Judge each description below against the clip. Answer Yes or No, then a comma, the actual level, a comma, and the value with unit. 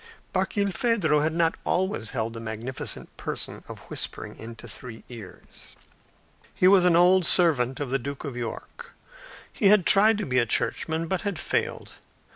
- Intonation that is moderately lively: No, wide, 7.3 semitones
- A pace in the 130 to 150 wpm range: No, average, 160 wpm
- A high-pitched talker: No, medium, 155 Hz